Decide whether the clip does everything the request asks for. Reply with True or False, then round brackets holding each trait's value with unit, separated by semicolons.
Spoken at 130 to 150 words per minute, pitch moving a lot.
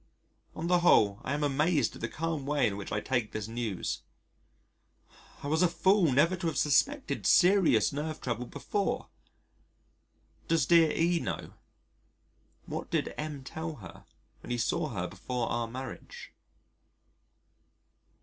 True (145 wpm; 5.8 semitones)